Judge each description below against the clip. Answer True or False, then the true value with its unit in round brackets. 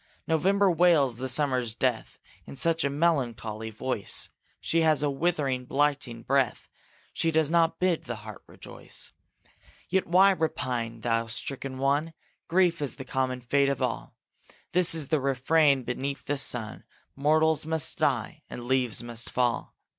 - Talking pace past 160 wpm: False (145 wpm)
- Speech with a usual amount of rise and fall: True (4.5 semitones)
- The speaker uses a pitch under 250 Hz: True (140 Hz)